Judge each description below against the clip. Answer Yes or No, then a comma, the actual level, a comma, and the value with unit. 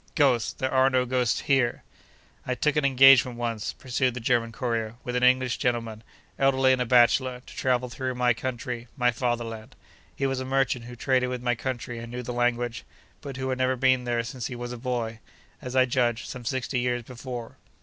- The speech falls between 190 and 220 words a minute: Yes, average, 200 wpm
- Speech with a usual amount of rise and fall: No, narrow, 1.5 semitones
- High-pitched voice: No, low, 125 Hz